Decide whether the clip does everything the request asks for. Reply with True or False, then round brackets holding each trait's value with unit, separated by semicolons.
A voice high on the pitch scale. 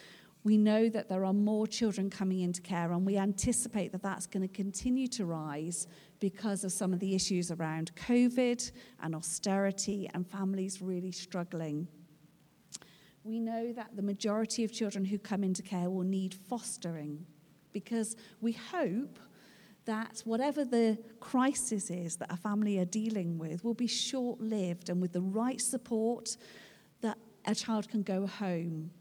True (200 Hz)